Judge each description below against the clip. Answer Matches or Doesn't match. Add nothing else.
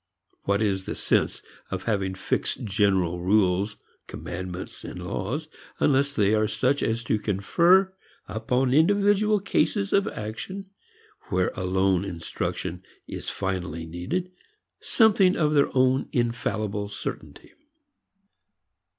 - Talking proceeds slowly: Matches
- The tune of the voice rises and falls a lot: Matches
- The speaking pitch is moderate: Doesn't match